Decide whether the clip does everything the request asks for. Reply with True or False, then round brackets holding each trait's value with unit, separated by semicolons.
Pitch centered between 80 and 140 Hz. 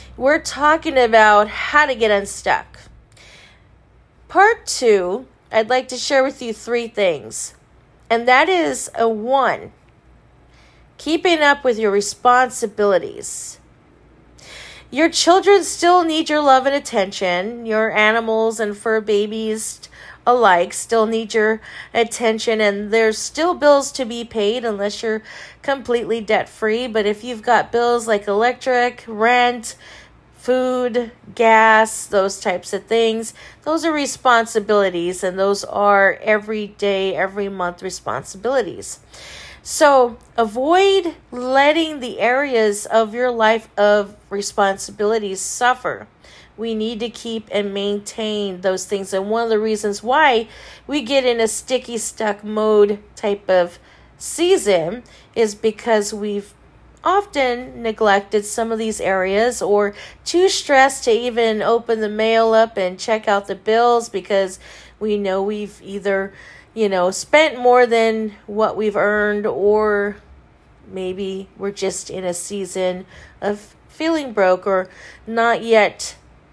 False (220 Hz)